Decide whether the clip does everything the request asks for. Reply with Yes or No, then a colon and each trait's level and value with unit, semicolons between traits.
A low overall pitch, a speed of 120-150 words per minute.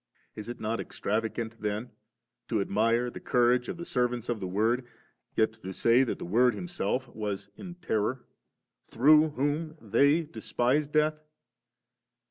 Yes: low, 120 Hz; average, 145 wpm